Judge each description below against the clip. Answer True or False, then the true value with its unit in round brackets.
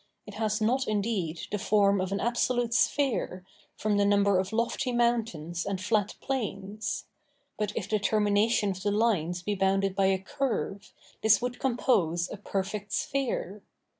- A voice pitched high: True (205 Hz)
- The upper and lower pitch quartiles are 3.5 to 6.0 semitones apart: False (3.0 semitones)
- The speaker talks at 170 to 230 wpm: False (160 wpm)